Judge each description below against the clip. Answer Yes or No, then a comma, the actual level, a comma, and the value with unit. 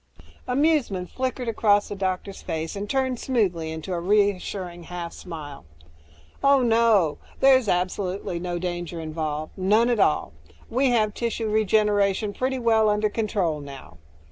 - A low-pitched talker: No, high, 200 Hz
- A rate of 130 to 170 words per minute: Yes, slow, 135 wpm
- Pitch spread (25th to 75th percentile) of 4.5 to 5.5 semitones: Yes, average, 4.8 semitones